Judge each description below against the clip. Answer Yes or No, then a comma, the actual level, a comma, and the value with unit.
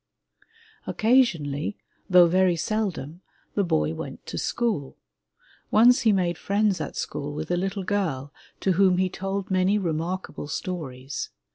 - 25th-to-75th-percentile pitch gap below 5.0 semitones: Yes, average, 4.2 semitones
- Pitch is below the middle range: No, medium, 185 Hz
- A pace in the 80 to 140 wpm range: Yes, slow, 135 wpm